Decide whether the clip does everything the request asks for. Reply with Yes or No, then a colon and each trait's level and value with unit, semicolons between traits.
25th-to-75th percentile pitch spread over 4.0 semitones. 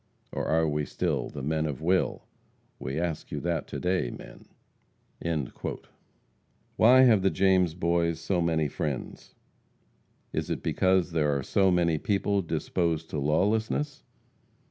No: average, 3.4 semitones